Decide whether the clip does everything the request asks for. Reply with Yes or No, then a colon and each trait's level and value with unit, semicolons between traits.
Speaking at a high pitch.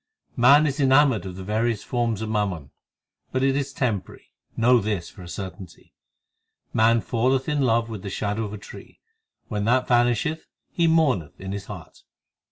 No: low, 115 Hz